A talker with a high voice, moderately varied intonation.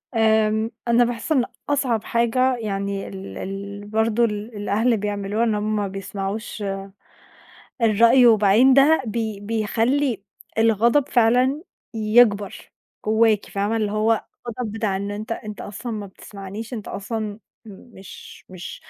No: high, 220 Hz; narrow, 2.3 semitones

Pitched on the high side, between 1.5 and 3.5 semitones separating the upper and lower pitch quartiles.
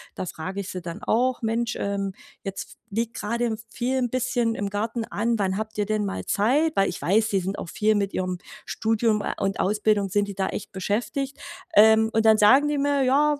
Yes: high, 215 Hz; average, 3.0 semitones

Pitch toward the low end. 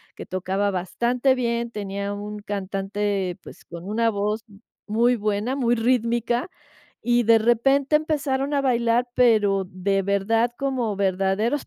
No: high, 225 Hz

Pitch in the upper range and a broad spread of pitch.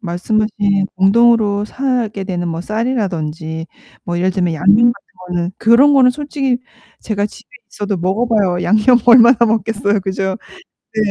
No: high, 205 Hz; average, 4.1 semitones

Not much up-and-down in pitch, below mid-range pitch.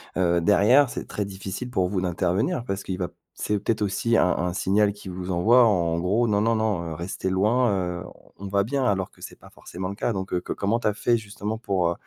No: average, 3.3 semitones; low, 100 Hz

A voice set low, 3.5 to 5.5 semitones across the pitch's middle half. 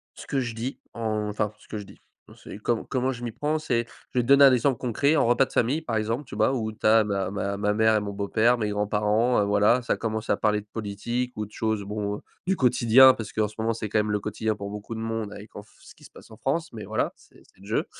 No: low, 110 Hz; average, 2.7 semitones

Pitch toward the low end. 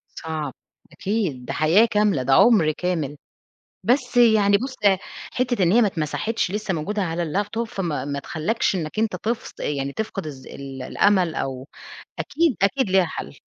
No: medium, 185 Hz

